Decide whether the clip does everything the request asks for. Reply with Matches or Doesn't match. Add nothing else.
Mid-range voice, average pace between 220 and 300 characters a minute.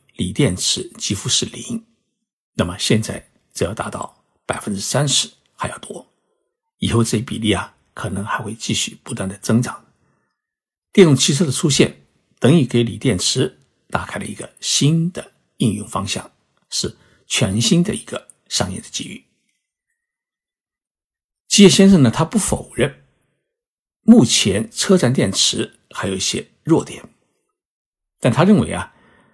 Doesn't match